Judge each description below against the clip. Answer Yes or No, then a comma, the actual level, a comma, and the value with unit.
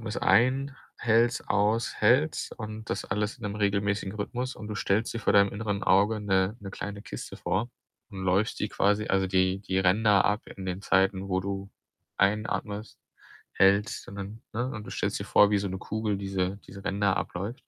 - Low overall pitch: Yes, low, 100 Hz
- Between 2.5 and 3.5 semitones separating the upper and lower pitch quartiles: No, narrow, 1.8 semitones